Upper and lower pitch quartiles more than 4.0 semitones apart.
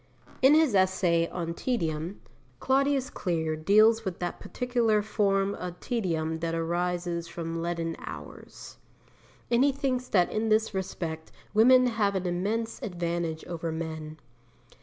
Yes: average, 5.1 semitones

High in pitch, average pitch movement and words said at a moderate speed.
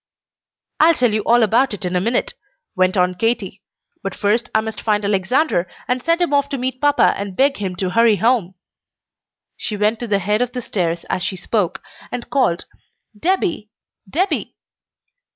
Yes: high, 220 Hz; average, 4.9 semitones; average, 180 wpm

